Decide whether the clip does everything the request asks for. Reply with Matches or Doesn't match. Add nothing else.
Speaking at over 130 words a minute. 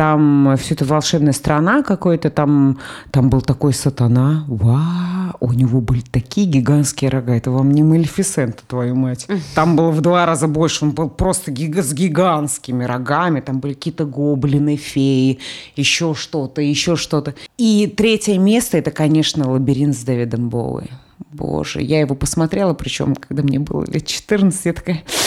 Matches